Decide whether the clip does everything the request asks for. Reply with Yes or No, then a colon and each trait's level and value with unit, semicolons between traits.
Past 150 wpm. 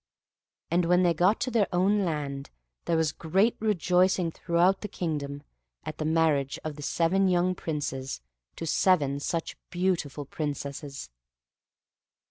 No: slow, 135 wpm